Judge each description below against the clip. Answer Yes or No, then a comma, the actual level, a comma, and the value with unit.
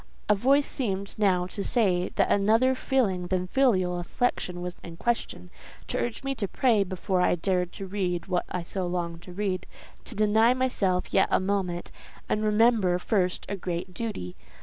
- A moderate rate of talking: Yes, average, 170 wpm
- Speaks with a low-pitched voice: No, high, 195 Hz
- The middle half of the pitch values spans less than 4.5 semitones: Yes, average, 3.6 semitones